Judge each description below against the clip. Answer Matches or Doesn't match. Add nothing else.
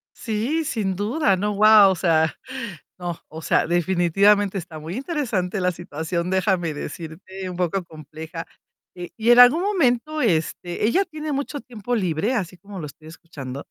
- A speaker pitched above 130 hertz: Matches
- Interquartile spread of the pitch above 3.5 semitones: Matches